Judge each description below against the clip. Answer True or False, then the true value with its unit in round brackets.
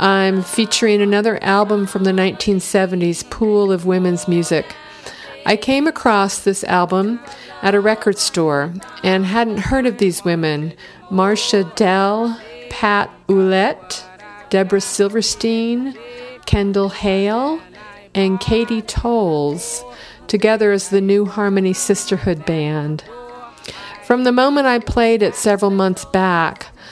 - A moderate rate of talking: False (120 wpm)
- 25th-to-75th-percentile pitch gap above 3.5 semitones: False (2.7 semitones)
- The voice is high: True (200 Hz)